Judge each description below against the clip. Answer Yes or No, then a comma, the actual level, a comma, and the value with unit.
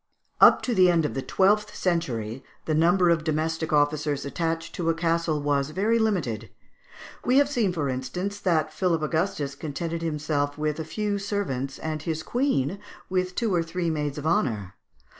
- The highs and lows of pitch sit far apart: No, average, 3.8 semitones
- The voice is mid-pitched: Yes, medium, 160 Hz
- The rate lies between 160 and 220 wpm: Yes, average, 175 wpm